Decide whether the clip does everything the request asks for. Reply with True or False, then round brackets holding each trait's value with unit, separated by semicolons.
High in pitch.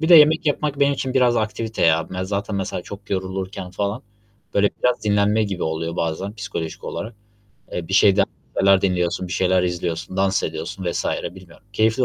False (100 Hz)